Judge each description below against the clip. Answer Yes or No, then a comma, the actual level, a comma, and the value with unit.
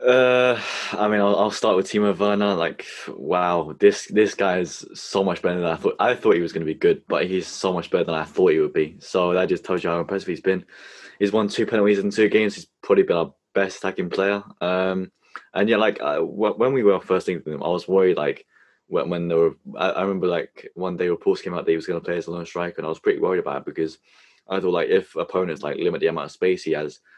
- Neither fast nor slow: No, fast, 275 wpm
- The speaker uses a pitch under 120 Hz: Yes, low, 105 Hz